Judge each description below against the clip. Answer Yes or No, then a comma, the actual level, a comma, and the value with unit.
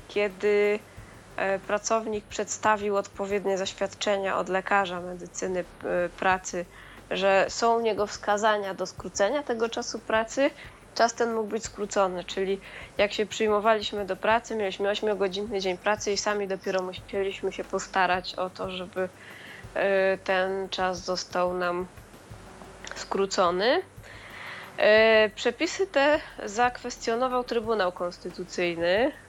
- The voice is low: No, high, 200 Hz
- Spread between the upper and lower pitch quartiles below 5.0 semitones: Yes, average, 2.8 semitones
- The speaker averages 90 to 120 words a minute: Yes, slow, 110 wpm